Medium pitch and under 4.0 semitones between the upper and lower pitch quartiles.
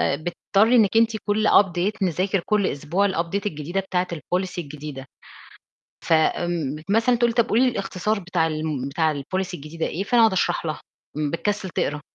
No: medium, 180 Hz; average, 4.8 semitones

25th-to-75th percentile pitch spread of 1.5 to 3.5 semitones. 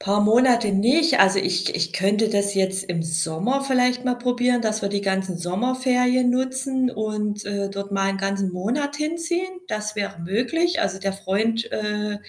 No: average, 4.3 semitones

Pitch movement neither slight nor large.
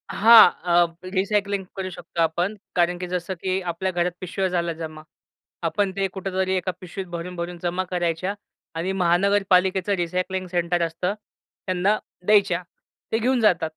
No: narrow, 1.9 semitones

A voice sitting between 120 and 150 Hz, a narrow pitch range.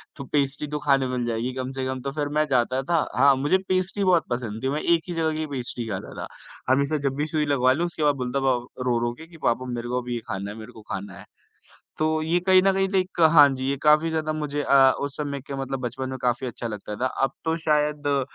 No: medium, 140 Hz; average, 3.5 semitones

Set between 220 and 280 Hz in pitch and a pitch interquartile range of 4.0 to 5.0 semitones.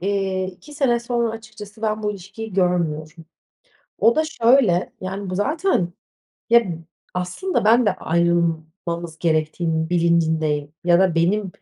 No: medium, 185 Hz; average, 4.6 semitones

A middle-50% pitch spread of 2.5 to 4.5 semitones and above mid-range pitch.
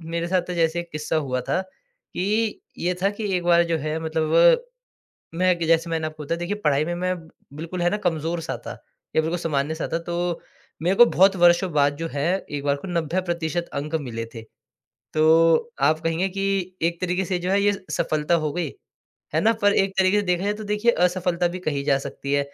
No: average, 2.8 semitones; medium, 170 Hz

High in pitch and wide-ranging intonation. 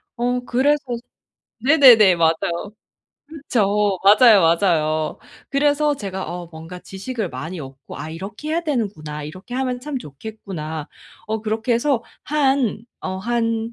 Yes: high, 215 Hz; wide, 6.7 semitones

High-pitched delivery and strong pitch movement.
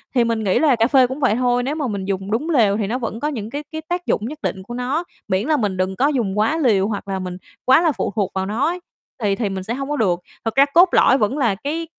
Yes: high, 235 Hz; wide, 6.0 semitones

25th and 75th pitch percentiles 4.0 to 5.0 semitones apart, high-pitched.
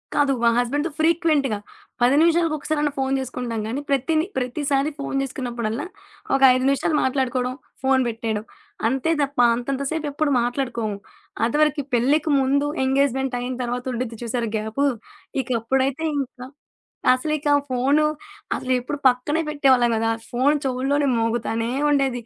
No: average, 2.9 semitones; very high, 265 Hz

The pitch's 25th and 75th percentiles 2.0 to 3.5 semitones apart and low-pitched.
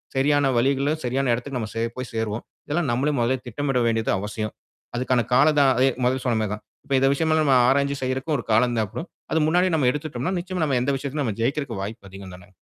No: average, 3.9 semitones; low, 130 Hz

